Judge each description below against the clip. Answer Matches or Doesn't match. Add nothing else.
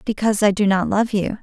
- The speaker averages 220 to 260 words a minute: Matches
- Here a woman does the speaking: Matches